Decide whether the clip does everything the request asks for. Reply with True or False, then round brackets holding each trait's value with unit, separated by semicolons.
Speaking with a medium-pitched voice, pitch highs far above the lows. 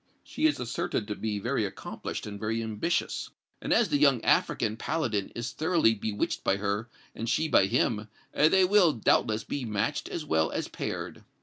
False (115 Hz; 6.5 semitones)